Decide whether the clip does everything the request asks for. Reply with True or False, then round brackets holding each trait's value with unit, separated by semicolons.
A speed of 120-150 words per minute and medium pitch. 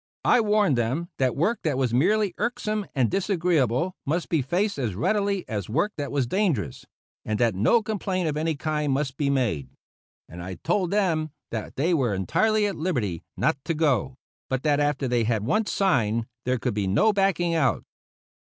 False (185 wpm; 150 Hz)